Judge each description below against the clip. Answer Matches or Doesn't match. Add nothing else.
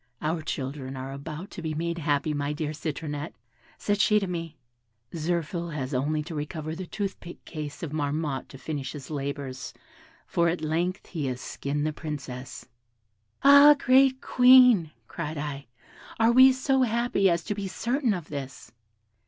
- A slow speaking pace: Doesn't match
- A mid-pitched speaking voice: Matches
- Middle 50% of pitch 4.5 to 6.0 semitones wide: Matches